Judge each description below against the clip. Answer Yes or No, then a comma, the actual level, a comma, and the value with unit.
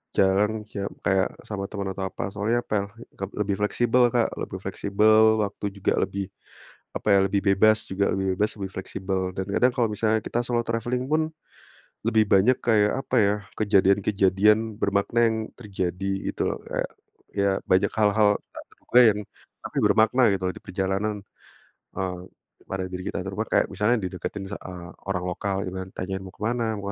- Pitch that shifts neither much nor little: No, narrow, 2.3 semitones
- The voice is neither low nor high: No, low, 100 Hz